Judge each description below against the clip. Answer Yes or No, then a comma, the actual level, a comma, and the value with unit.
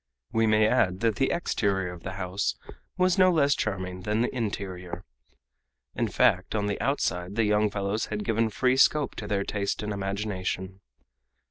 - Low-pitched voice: Yes, low, 105 Hz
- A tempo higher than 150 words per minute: Yes, average, 170 wpm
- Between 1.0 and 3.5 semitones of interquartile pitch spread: Yes, average, 3.1 semitones